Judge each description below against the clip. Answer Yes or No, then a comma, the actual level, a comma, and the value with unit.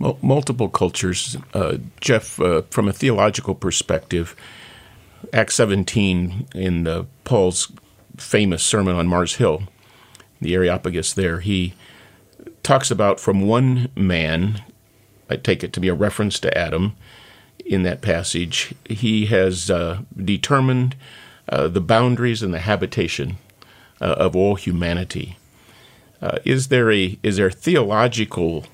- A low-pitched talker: Yes, low, 100 Hz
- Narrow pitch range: No, average, 3.5 semitones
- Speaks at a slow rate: Yes, slow, 130 wpm